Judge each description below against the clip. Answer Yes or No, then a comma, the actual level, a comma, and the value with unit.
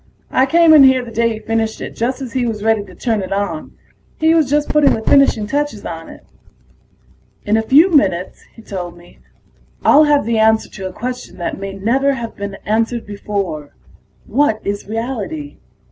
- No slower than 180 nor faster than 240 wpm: Yes, average, 190 wpm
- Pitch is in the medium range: No, high, 225 Hz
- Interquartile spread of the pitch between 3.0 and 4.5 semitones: No, average, 5.1 semitones